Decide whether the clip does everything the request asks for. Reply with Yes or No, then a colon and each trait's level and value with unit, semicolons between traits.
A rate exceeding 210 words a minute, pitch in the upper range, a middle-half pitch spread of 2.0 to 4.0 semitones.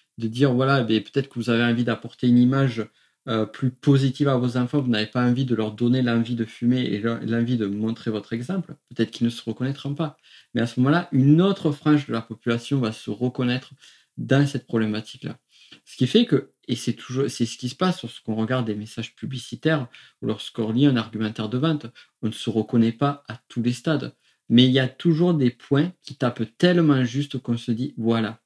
No: fast, 220 wpm; low, 125 Hz; average, 3.1 semitones